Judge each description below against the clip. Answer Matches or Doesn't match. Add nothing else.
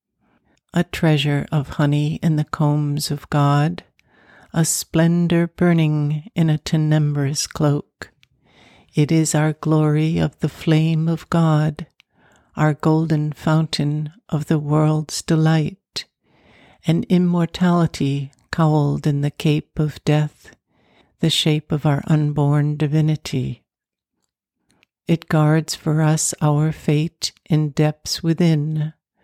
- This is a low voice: Doesn't match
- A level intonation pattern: Matches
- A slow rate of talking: Matches